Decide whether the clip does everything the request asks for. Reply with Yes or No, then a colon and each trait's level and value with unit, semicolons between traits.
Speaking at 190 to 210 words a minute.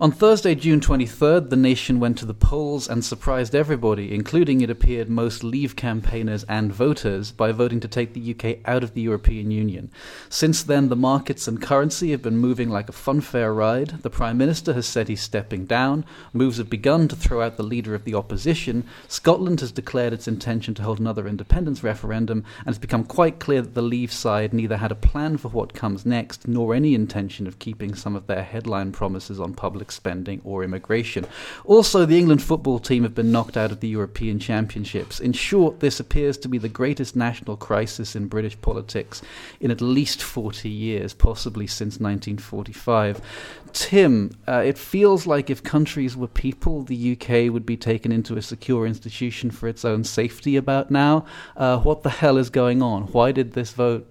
Yes: average, 195 wpm